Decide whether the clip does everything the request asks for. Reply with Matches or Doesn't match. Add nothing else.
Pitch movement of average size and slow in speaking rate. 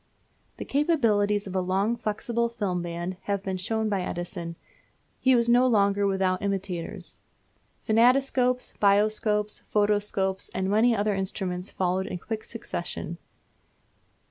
Matches